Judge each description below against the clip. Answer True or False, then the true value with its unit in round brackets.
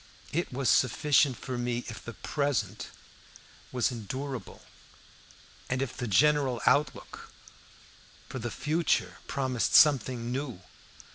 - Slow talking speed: True (115 wpm)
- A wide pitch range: False (3.0 semitones)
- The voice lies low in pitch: True (130 Hz)